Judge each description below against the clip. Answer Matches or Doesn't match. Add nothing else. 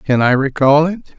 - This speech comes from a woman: Doesn't match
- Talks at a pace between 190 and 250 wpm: Matches